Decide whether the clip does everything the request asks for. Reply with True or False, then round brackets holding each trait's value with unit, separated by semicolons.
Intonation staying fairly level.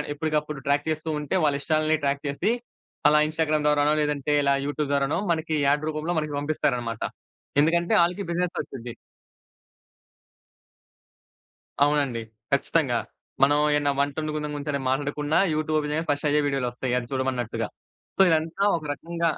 True (1.8 semitones)